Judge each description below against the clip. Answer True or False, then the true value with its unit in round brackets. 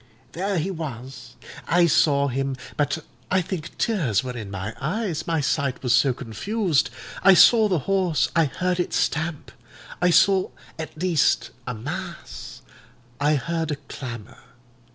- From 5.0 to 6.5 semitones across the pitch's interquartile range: True (5.3 semitones)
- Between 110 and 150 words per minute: True (145 wpm)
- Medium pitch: True (155 Hz)